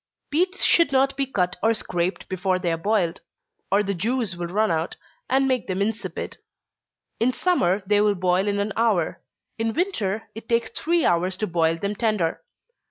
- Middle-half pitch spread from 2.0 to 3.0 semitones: No, average, 4.3 semitones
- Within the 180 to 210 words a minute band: Yes, average, 185 wpm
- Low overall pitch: No, high, 205 Hz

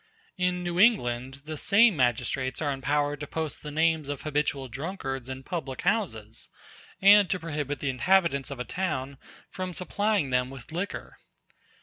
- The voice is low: No, medium, 150 Hz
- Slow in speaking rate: No, average, 155 wpm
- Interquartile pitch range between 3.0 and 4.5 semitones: No, average, 5.3 semitones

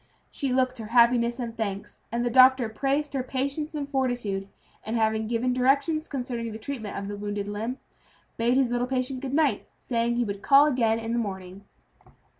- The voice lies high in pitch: Yes, high, 240 Hz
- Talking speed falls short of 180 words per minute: No, average, 190 wpm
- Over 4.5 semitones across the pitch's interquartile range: No, average, 3.1 semitones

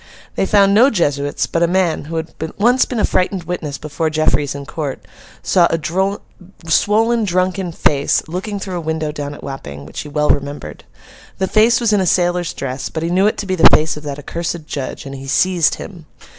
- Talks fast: Yes, fast, 210 wpm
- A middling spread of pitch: Yes, average, 4.5 semitones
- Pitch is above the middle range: No, medium, 165 Hz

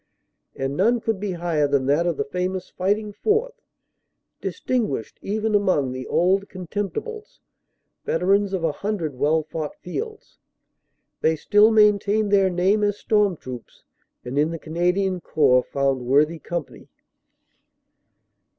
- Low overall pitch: No, medium, 185 Hz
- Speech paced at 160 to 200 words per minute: No, slow, 135 wpm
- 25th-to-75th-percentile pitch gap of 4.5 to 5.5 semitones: Yes, average, 5.2 semitones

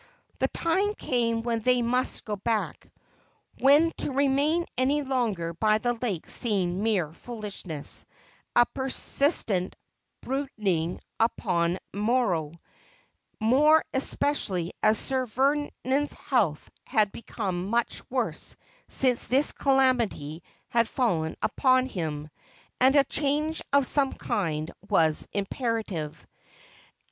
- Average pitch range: No, wide, 6.2 semitones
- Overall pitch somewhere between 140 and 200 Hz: No, high, 235 Hz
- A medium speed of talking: No, slow, 110 wpm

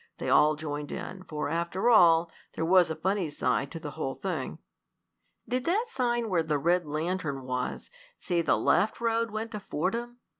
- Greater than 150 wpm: Yes, average, 180 wpm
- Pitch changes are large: Yes, wide, 6.1 semitones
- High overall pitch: No, medium, 175 Hz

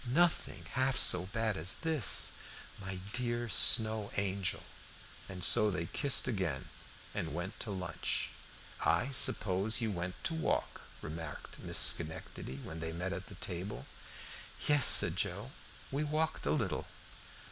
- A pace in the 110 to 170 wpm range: Yes, slow, 135 wpm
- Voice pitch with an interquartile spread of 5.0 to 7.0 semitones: Yes, wide, 5.5 semitones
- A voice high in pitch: No, low, 100 Hz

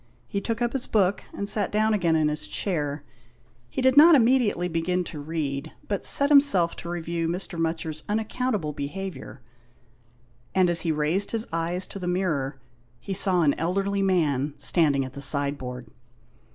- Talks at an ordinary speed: Yes, average, 170 wpm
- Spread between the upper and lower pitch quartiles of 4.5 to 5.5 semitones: Yes, average, 4.9 semitones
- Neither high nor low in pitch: Yes, medium, 175 Hz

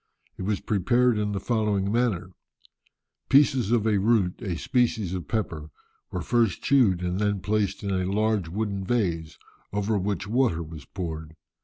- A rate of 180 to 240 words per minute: No, average, 160 wpm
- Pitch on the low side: Yes, low, 100 Hz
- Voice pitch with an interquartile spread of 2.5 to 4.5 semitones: Yes, average, 3.7 semitones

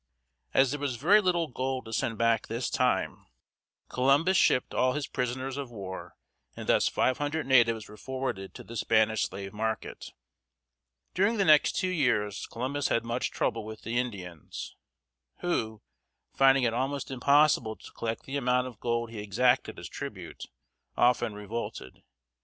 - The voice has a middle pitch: No, low, 125 Hz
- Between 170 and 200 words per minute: No, average, 160 wpm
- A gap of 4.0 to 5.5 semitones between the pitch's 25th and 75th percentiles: No, average, 3.6 semitones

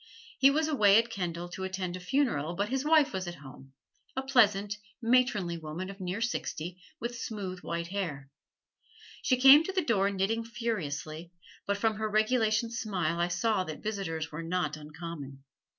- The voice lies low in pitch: No, high, 195 Hz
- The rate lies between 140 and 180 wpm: Yes, average, 170 wpm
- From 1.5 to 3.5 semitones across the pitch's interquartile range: No, average, 5.3 semitones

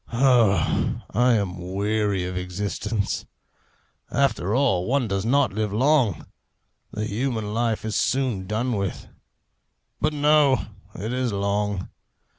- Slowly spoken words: Yes, slow, 120 wpm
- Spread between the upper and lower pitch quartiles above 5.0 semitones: No, average, 4.2 semitones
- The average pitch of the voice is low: Yes, low, 110 Hz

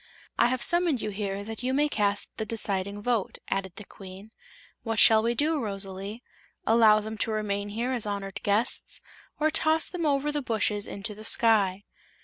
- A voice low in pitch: No, high, 215 Hz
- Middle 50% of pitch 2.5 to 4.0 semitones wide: Yes, average, 3.4 semitones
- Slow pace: No, average, 180 wpm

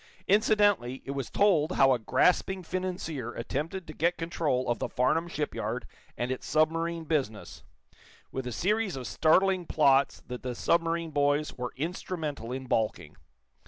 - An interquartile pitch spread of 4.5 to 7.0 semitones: Yes, average, 5.1 semitones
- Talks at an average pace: Yes, average, 150 wpm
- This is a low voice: No, medium, 155 Hz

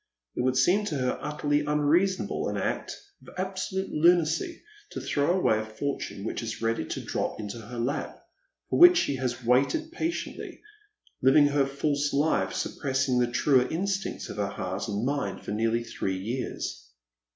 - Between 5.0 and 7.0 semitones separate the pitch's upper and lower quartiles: Yes, wide, 5.5 semitones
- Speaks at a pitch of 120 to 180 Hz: Yes, medium, 140 Hz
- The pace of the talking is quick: No, average, 165 wpm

